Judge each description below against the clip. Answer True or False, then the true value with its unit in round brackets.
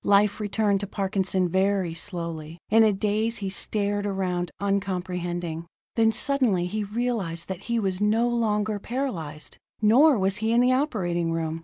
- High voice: True (200 Hz)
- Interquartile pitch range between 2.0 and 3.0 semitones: False (3.7 semitones)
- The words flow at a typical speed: True (155 wpm)